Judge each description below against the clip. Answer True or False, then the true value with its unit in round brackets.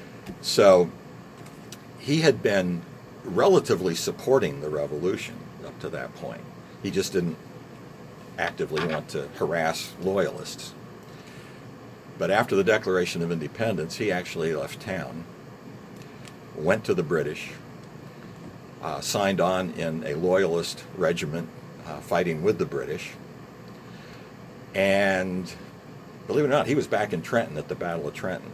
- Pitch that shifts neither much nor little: False (1.9 semitones)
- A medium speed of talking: False (130 wpm)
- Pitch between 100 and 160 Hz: False (90 Hz)